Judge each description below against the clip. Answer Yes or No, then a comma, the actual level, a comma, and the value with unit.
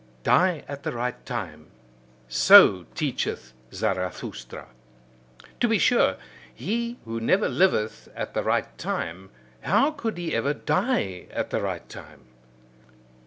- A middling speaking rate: No, slow, 125 wpm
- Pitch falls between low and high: Yes, medium, 155 Hz